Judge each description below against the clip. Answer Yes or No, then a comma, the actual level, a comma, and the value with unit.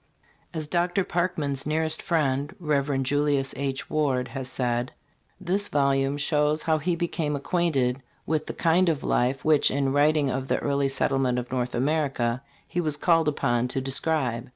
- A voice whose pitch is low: No, medium, 145 Hz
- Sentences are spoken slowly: No, average, 160 wpm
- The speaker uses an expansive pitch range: No, average, 3.0 semitones